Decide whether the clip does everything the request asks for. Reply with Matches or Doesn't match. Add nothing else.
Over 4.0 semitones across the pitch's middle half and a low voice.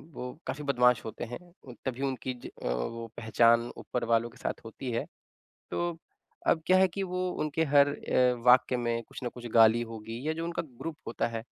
Matches